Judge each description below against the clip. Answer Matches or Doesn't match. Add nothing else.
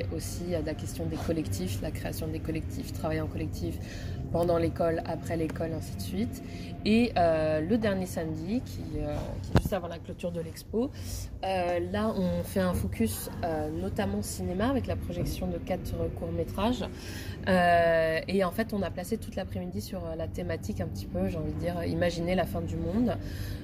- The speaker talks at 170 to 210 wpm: Matches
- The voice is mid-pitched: Doesn't match